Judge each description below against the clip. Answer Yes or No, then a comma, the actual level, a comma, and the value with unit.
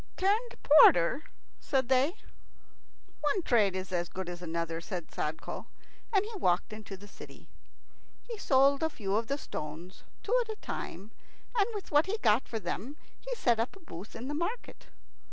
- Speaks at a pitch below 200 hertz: No, high, 240 Hz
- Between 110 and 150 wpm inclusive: No, average, 175 wpm